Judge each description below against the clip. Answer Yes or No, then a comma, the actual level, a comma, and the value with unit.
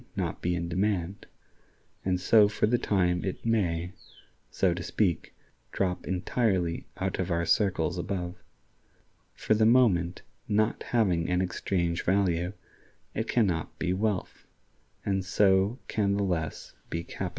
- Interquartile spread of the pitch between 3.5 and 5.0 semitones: No, average, 2.8 semitones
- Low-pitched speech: Yes, very low, 95 Hz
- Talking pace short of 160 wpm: Yes, average, 140 wpm